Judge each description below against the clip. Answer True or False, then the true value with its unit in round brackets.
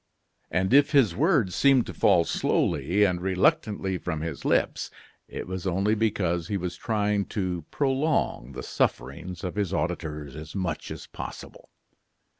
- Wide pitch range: False (4.1 semitones)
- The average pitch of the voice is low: True (95 Hz)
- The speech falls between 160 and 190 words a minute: False (150 wpm)